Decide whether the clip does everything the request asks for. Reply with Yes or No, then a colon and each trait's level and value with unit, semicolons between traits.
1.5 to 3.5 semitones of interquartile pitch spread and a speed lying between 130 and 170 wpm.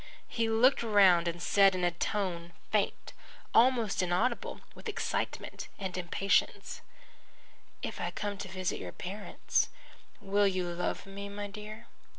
Yes: average, 2.7 semitones; average, 140 wpm